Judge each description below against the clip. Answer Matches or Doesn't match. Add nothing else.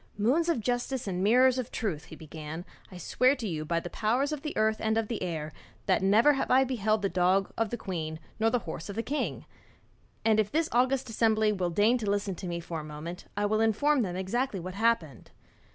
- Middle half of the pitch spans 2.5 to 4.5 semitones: Doesn't match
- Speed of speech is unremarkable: Doesn't match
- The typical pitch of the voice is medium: Doesn't match